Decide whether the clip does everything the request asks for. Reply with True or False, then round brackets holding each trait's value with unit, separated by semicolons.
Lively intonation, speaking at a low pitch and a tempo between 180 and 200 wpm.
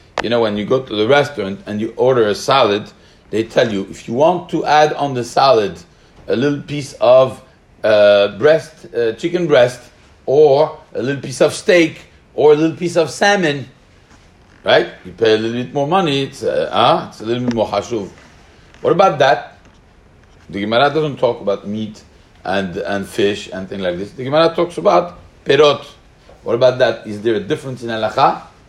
True (6.7 semitones; 130 Hz; 190 wpm)